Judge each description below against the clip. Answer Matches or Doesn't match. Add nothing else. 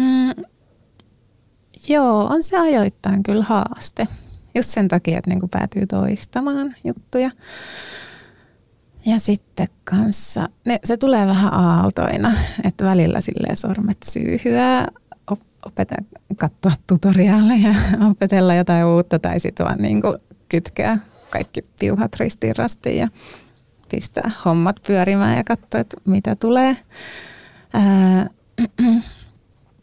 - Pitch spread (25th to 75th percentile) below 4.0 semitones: Doesn't match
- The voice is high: Matches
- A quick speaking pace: Doesn't match